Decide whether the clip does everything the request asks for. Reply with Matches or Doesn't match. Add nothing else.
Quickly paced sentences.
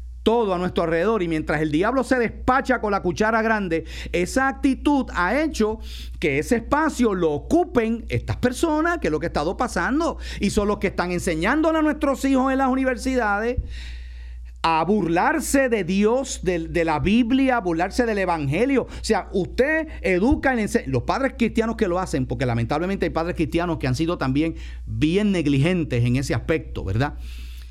Doesn't match